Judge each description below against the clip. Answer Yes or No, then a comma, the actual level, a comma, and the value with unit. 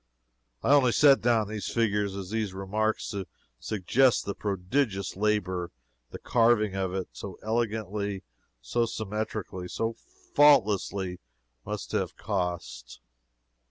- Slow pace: Yes, slow, 120 wpm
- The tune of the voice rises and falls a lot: No, average, 2.9 semitones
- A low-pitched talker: Yes, low, 105 Hz